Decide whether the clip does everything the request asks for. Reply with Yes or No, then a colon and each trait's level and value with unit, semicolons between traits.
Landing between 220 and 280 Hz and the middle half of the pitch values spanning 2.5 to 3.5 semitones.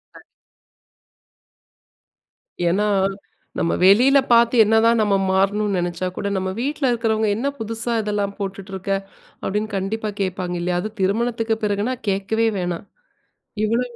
No: high, 210 Hz; average, 2.9 semitones